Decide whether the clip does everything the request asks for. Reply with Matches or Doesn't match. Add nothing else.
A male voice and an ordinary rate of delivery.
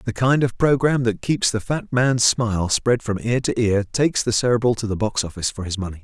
Doesn't match